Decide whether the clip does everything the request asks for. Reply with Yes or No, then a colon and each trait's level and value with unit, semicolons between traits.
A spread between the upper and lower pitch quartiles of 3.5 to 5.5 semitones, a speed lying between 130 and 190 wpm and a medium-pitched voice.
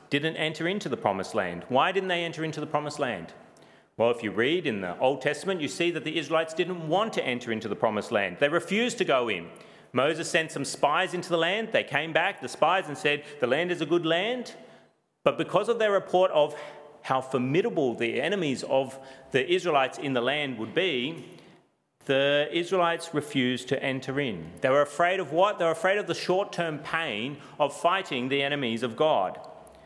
No: average, 4.3 semitones; fast, 205 wpm; medium, 155 Hz